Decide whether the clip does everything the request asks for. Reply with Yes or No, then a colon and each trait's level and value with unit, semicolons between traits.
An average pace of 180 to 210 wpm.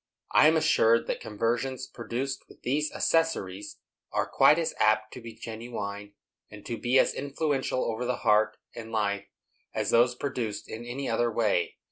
No: average, 165 wpm